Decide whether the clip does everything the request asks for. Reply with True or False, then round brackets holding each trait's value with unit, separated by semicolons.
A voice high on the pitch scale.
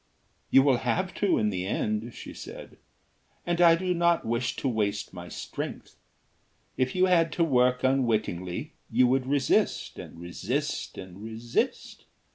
False (125 Hz)